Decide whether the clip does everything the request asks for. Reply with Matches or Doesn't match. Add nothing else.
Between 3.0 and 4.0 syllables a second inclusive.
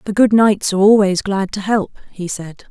Doesn't match